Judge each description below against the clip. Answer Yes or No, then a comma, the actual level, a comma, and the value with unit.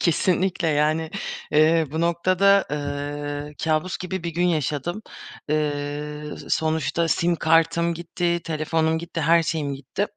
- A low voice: No, medium, 160 Hz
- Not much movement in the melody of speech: Yes, narrow, 2.3 semitones